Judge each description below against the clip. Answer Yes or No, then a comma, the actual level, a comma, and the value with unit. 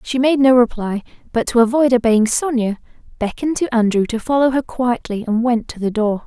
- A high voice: Yes, high, 240 Hz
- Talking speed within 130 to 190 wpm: No, average, 200 wpm